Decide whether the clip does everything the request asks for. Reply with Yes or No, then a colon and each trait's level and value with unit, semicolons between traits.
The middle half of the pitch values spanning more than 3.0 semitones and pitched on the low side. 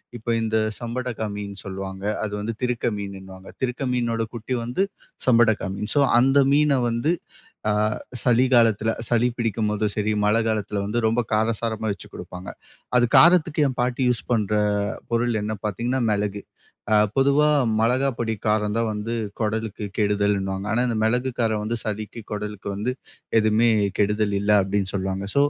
No: average, 2.7 semitones; low, 110 Hz